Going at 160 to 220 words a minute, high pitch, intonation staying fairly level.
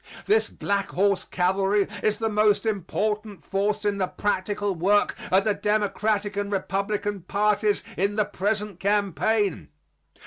No: slow, 135 wpm; high, 205 Hz; narrow, 1.2 semitones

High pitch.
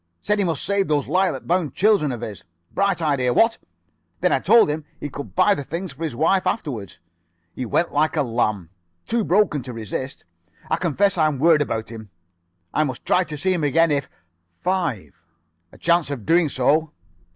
No: medium, 155 Hz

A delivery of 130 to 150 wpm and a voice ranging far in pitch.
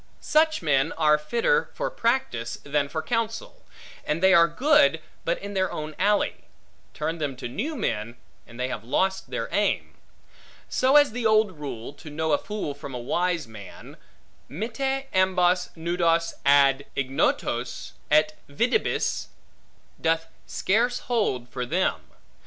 Yes: average, 145 wpm; wide, 7.4 semitones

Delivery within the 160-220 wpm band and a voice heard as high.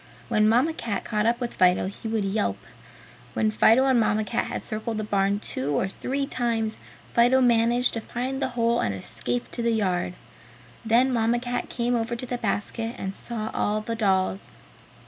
Yes: average, 185 wpm; high, 225 Hz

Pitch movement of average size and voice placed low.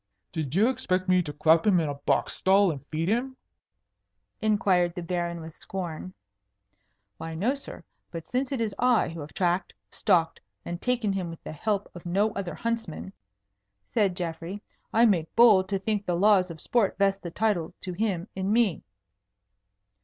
No: average, 4.0 semitones; medium, 185 Hz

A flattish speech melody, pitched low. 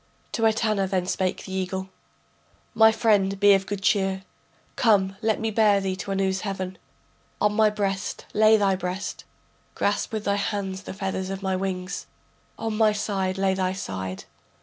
No: narrow, 1.8 semitones; high, 195 Hz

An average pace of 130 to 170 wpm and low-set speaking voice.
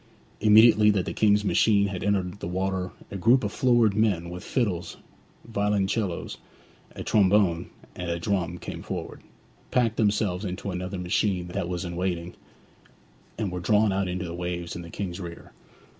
Yes: average, 165 wpm; very low, 95 Hz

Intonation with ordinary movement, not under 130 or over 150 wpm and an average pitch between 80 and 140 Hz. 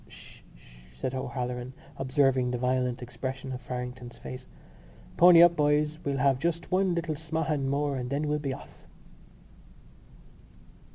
Yes: average, 3.1 semitones; average, 145 wpm; low, 135 Hz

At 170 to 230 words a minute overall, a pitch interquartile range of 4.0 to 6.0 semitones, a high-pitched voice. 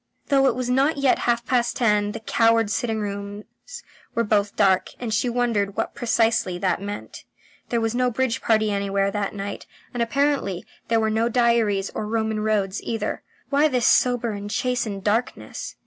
No: average, 175 wpm; average, 2.9 semitones; high, 225 Hz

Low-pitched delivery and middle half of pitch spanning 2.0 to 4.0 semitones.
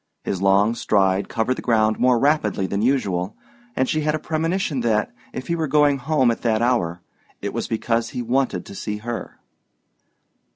No: low, 120 Hz; average, 4.7 semitones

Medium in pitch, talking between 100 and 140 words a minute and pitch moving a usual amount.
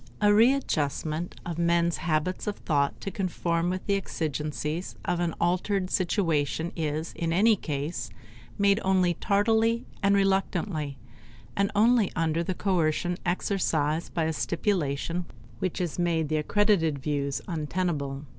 Yes: medium, 170 Hz; slow, 135 wpm; average, 3.9 semitones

